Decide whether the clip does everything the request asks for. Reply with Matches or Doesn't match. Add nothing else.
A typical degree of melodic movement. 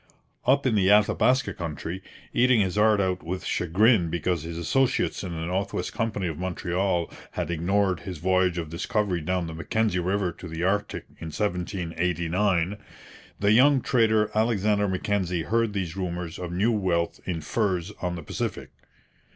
Matches